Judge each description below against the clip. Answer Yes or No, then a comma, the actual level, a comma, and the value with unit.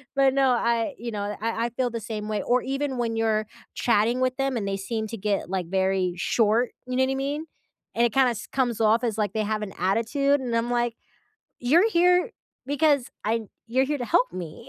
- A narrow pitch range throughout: No, average, 3.6 semitones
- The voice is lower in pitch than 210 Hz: No, high, 235 Hz